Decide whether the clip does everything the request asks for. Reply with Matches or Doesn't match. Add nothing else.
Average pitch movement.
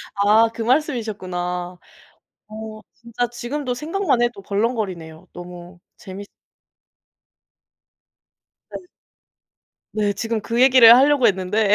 Matches